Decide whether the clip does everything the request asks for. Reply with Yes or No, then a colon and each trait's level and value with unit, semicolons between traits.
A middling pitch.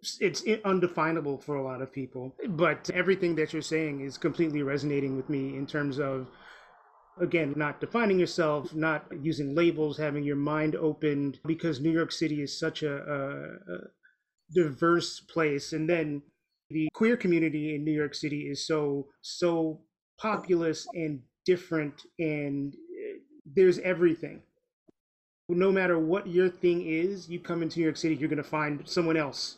Yes: medium, 160 Hz